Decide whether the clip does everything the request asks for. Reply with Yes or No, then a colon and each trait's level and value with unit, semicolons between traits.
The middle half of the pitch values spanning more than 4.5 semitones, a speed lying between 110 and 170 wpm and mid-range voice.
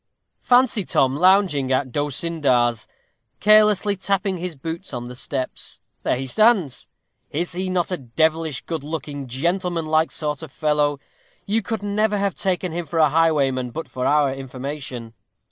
Yes: wide, 5.4 semitones; average, 150 wpm; medium, 160 Hz